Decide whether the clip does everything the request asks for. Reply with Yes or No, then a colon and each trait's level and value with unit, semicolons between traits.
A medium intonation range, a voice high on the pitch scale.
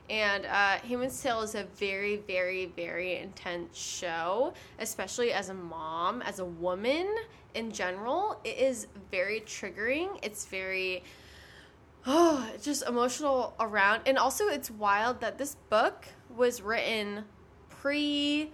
No: wide, 6.1 semitones; high, 220 Hz